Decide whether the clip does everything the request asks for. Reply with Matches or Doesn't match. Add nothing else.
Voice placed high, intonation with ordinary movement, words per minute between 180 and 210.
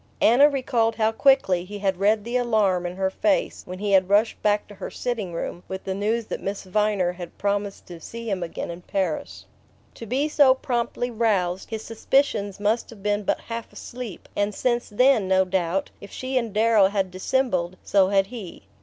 Matches